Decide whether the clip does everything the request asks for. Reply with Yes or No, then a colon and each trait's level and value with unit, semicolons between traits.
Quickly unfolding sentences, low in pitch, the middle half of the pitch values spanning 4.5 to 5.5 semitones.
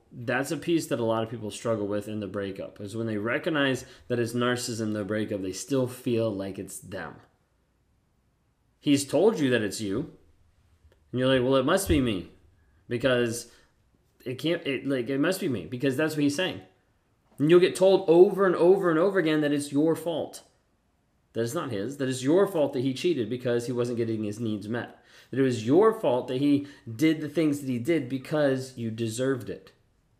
Yes: fast, 210 wpm; low, 125 Hz; average, 4.9 semitones